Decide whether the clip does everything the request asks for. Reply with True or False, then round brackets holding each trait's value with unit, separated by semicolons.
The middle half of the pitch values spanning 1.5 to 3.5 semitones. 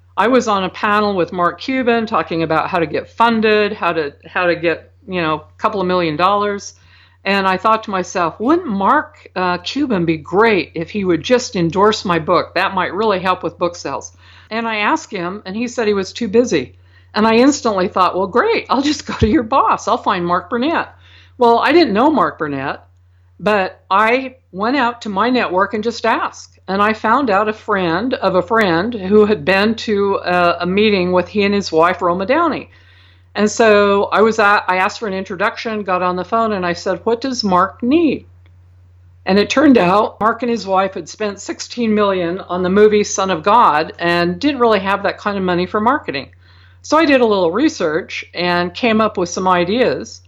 False (4.5 semitones)